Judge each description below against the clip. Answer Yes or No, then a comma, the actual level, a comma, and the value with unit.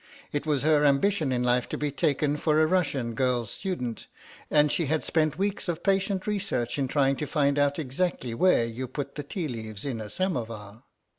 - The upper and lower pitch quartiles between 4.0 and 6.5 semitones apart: Yes, average, 4.3 semitones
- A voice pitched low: No, medium, 145 Hz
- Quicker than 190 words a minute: Yes, average, 200 wpm